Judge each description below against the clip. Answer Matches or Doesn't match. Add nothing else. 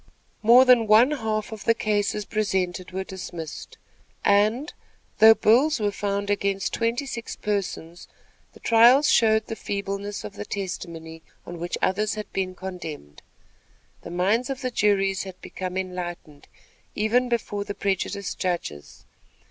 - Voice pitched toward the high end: Matches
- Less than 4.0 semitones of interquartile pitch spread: Matches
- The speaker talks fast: Doesn't match